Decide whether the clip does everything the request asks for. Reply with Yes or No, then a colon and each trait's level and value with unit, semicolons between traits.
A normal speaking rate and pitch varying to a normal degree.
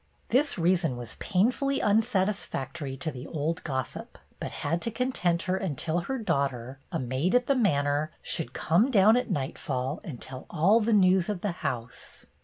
No: average, 170 wpm; wide, 7.1 semitones